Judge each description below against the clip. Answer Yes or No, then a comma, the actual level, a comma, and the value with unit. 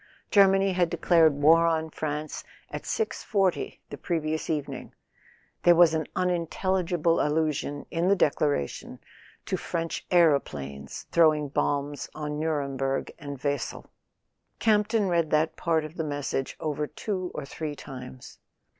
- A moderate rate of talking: No, slow, 130 wpm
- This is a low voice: No, medium, 155 Hz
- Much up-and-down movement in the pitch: No, average, 3.2 semitones